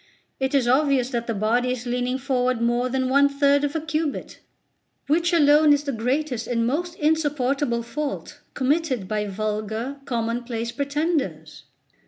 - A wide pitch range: No, average, 3.6 semitones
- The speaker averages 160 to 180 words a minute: No, average, 150 wpm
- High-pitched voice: Yes, very high, 260 Hz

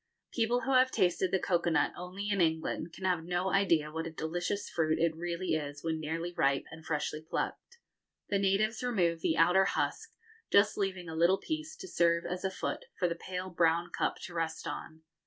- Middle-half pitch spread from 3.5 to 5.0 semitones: No, average, 3.1 semitones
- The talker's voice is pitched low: No, medium, 175 Hz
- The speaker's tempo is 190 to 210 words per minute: Yes, average, 200 wpm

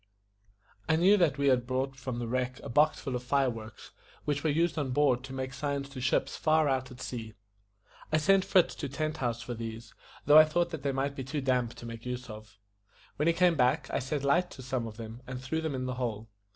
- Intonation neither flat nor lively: Yes, average, 3.3 semitones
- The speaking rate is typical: No, fast, 245 wpm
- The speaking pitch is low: Yes, low, 130 Hz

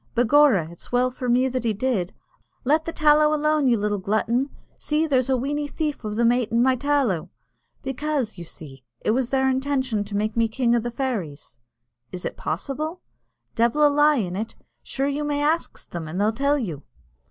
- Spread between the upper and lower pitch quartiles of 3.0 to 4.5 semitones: No, average, 5.0 semitones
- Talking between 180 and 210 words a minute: Yes, average, 195 wpm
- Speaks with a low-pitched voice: No, very high, 250 Hz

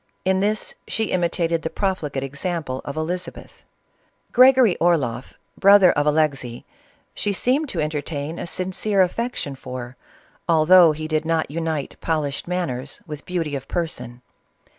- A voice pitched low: No, medium, 160 Hz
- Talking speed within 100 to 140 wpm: Yes, slow, 135 wpm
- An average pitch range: Yes, average, 4.2 semitones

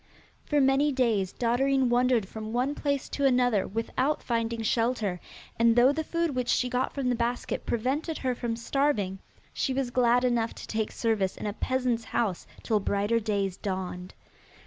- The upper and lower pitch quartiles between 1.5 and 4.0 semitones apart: Yes, average, 3.0 semitones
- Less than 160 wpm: No, average, 170 wpm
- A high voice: Yes, high, 240 Hz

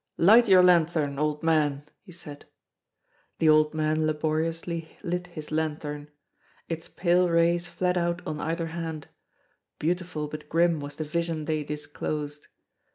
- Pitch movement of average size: No, narrow, 2.2 semitones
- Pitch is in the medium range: Yes, medium, 160 Hz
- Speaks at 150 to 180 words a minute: No, average, 140 wpm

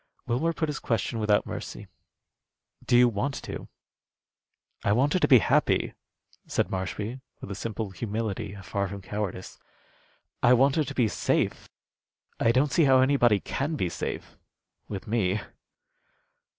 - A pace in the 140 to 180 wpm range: Yes, average, 150 wpm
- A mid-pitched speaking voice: No, low, 115 Hz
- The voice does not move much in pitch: No, average, 4.8 semitones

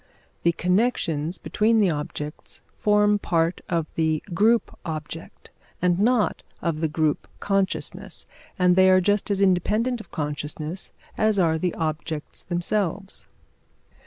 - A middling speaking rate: No, slow, 130 wpm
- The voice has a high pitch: No, medium, 180 Hz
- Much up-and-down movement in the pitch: No, average, 4.3 semitones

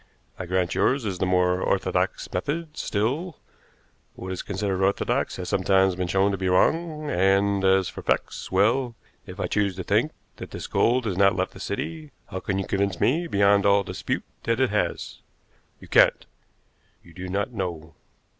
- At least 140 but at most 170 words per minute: No, average, 180 wpm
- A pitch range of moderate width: Yes, average, 3.9 semitones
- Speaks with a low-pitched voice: Yes, low, 100 Hz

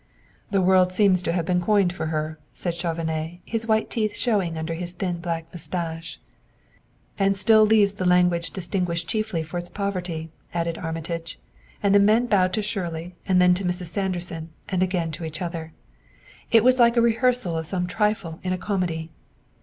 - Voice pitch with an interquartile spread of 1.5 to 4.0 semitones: Yes, average, 3.2 semitones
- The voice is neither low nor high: Yes, medium, 180 Hz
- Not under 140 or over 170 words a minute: No, average, 180 wpm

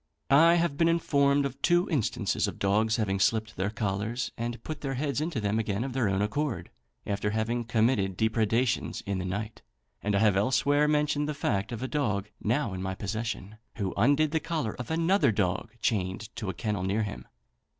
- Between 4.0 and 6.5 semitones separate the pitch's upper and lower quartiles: Yes, wide, 5.6 semitones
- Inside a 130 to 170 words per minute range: No, average, 195 wpm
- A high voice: No, low, 115 Hz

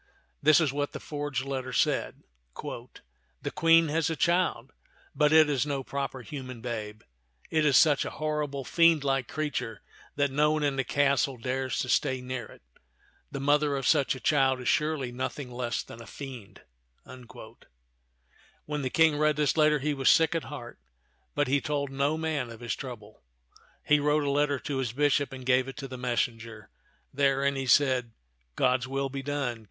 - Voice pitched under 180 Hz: Yes, low, 135 Hz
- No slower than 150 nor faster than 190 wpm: Yes, average, 185 wpm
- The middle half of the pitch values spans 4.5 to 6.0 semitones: No, average, 2.8 semitones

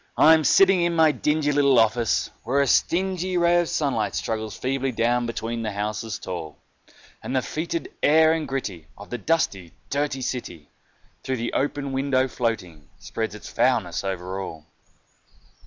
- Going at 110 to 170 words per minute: Yes, average, 160 wpm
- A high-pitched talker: No, low, 125 Hz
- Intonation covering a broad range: Yes, wide, 5.9 semitones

